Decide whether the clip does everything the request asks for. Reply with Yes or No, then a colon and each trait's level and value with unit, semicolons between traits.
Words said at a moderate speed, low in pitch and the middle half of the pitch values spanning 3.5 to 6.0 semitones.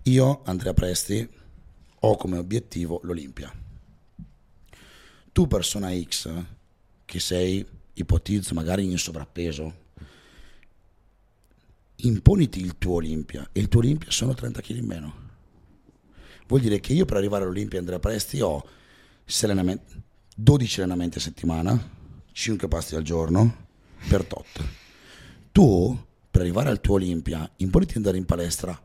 Yes: average, 125 wpm; very low, 95 Hz; average, 3.9 semitones